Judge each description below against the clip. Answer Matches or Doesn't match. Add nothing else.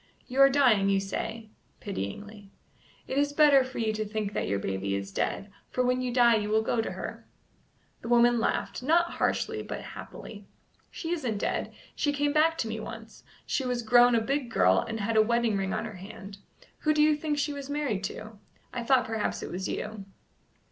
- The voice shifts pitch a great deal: Doesn't match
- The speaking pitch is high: Matches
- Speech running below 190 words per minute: Doesn't match